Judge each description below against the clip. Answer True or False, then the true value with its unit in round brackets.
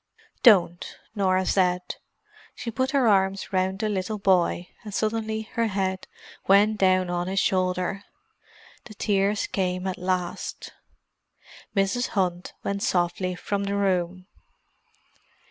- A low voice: False (190 Hz)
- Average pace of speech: False (120 wpm)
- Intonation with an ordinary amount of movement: False (2.0 semitones)